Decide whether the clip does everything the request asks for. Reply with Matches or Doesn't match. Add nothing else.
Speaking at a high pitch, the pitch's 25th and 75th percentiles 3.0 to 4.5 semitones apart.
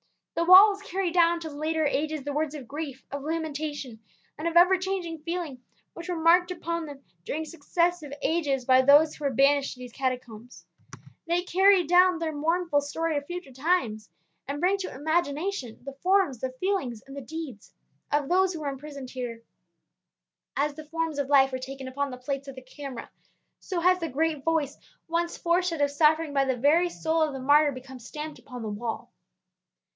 Matches